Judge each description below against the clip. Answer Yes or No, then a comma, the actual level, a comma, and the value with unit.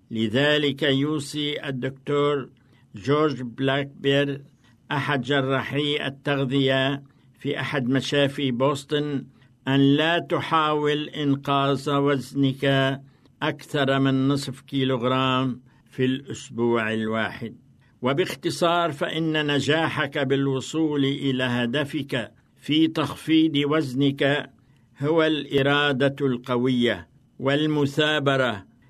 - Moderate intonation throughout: No, narrow, 2.0 semitones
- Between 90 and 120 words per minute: No, average, 75 wpm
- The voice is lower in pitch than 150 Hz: Yes, medium, 140 Hz